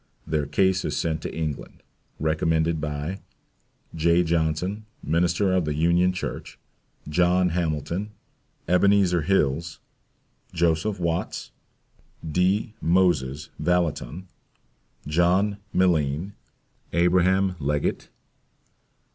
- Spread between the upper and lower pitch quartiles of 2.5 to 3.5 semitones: Yes, average, 2.8 semitones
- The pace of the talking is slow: Yes, slow, 90 wpm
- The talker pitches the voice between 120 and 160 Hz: No, very low, 85 Hz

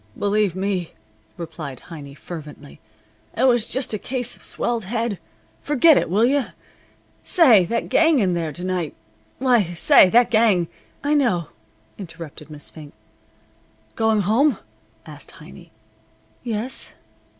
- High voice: Yes, high, 200 Hz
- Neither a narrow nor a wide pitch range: No, wide, 6.1 semitones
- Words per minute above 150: No, slow, 135 wpm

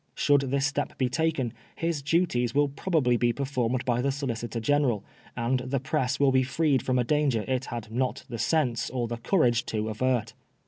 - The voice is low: Yes, low, 130 Hz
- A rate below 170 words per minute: No, average, 190 wpm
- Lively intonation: No, average, 3.2 semitones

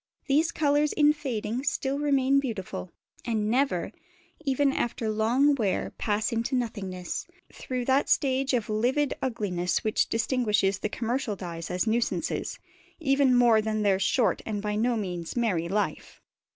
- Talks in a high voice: Yes, high, 230 Hz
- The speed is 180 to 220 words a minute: No, average, 145 wpm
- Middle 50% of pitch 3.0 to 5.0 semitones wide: Yes, average, 4.3 semitones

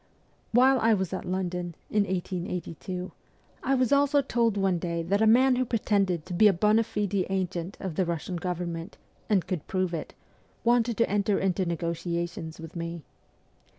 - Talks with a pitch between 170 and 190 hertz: Yes, medium, 185 Hz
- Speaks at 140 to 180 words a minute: Yes, average, 170 wpm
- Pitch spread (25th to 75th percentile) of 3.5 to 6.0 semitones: Yes, average, 3.9 semitones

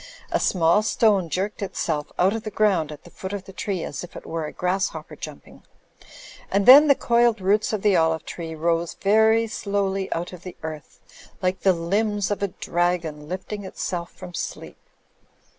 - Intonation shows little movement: No, average, 3.4 semitones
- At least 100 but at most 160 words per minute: No, average, 185 wpm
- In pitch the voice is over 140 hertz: Yes, high, 190 Hz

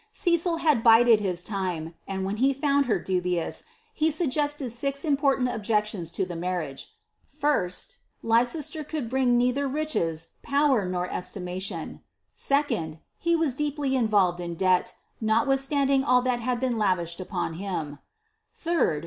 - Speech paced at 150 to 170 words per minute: No, average, 140 wpm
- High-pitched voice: Yes, high, 235 Hz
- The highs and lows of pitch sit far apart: Yes, wide, 7.4 semitones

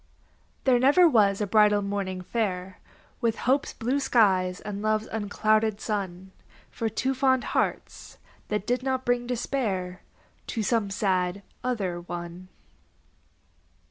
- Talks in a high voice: Yes, high, 210 Hz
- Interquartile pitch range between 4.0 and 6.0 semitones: Yes, average, 4.3 semitones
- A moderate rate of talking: No, slow, 125 wpm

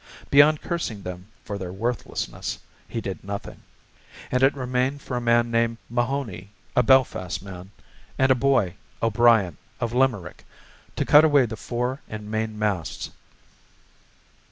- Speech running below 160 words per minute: Yes, average, 140 wpm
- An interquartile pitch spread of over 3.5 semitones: Yes, average, 4.5 semitones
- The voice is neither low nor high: No, low, 115 Hz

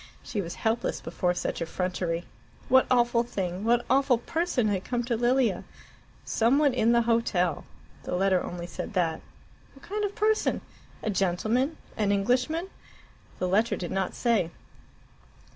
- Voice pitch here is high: Yes, high, 225 Hz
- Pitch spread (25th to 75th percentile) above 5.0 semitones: Yes, wide, 5.4 semitones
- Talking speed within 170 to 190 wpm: No, average, 150 wpm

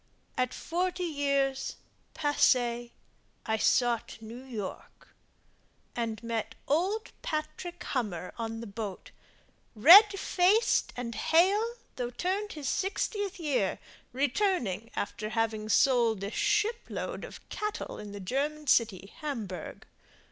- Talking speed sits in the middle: No, slow, 115 wpm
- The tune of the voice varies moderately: No, wide, 7.8 semitones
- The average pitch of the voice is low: No, very high, 260 Hz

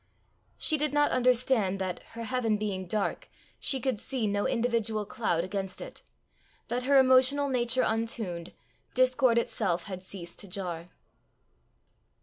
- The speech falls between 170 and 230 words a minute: No, slow, 135 wpm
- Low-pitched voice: No, high, 225 Hz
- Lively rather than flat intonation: No, average, 4.8 semitones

